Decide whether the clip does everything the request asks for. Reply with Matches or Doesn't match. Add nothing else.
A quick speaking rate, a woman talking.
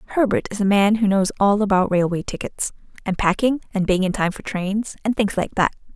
Matches